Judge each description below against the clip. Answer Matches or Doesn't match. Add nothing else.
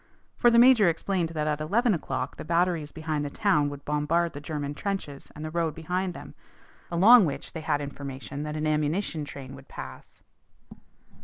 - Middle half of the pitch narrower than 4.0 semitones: Matches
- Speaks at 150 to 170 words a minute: Doesn't match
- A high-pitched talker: Doesn't match